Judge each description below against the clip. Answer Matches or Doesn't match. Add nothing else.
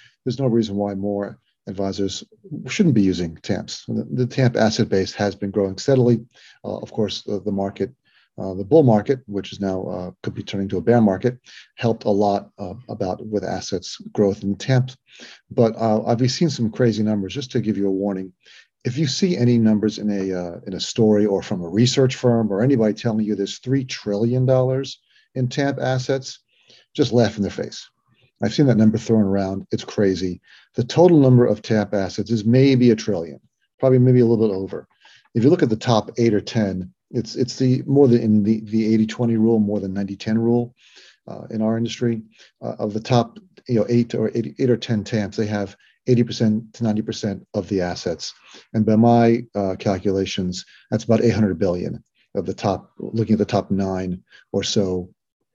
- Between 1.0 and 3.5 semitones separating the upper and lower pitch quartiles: Matches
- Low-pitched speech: Matches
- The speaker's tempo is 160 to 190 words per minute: Doesn't match